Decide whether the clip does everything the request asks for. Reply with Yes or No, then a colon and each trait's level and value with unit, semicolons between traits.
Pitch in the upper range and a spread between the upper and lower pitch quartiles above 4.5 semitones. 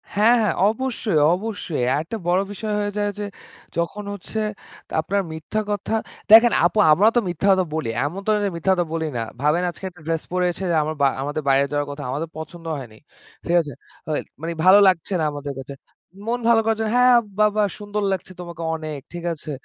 No: medium, 175 Hz; average, 4.9 semitones